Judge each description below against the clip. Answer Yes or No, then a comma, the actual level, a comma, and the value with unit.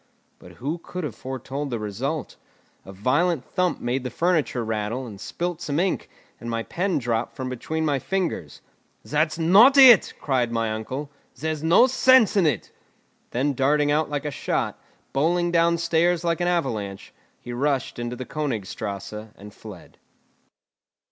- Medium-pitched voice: Yes, medium, 145 Hz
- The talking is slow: No, average, 160 wpm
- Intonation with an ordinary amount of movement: No, wide, 6.0 semitones